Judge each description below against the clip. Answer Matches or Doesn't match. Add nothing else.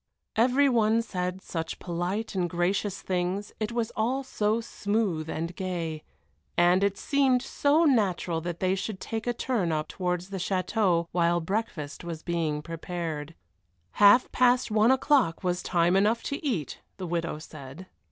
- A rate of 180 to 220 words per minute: Doesn't match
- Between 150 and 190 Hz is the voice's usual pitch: Matches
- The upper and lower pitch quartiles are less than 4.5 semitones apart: Doesn't match